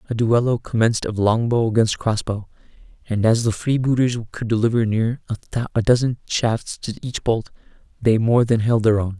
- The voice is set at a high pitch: No, low, 115 Hz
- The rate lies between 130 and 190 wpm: Yes, average, 170 wpm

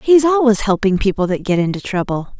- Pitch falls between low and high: No, high, 215 Hz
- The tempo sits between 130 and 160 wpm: No, average, 200 wpm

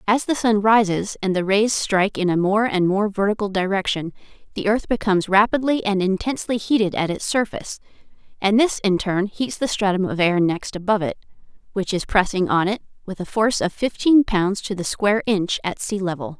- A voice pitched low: No, high, 200 Hz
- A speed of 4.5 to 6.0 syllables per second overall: Yes, 5.5 syllables/s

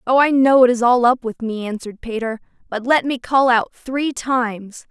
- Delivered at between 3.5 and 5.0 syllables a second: Yes, 4.9 syllables/s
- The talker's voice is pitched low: No, high, 245 Hz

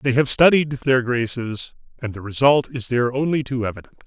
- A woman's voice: No, male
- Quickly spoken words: No, average, 190 wpm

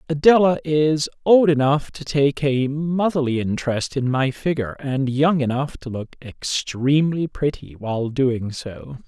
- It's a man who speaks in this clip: Yes, male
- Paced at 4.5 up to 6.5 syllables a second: No, 4.3 syllables/s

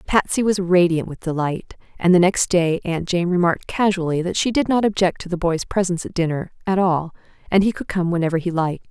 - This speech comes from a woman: Yes, female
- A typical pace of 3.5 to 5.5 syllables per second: No, 5.9 syllables/s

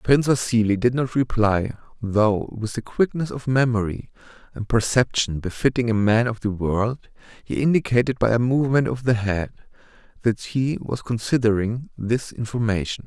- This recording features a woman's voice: No, male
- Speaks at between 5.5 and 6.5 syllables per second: No, 4.9 syllables/s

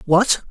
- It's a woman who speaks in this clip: Yes, female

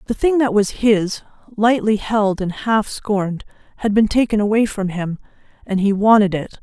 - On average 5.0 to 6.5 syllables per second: No, 4.8 syllables/s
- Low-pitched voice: No, high, 210 Hz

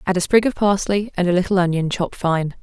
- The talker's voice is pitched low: No, medium, 185 Hz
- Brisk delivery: Yes, fast, 250 wpm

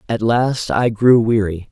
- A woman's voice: No, male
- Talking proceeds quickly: No, average, 175 wpm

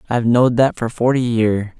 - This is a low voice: Yes, low, 120 Hz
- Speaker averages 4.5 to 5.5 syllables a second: No, 5.7 syllables/s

